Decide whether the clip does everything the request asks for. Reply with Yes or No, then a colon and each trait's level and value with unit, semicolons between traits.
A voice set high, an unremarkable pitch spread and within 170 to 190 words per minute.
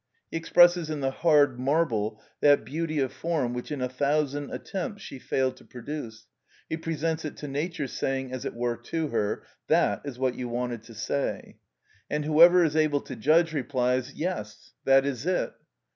No: medium, 140 Hz; average, 3.9 semitones; average, 180 wpm